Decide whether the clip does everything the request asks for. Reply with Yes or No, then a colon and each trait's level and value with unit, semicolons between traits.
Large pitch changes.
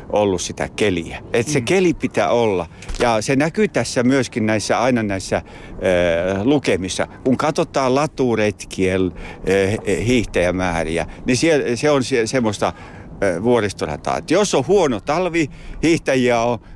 Yes: wide, 6.2 semitones